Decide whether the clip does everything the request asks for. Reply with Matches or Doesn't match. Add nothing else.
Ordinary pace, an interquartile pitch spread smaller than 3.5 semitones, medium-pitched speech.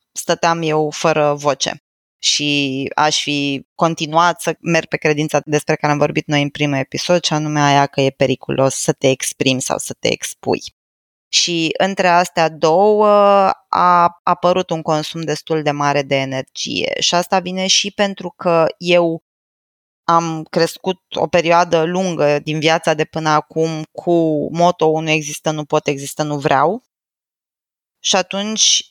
Matches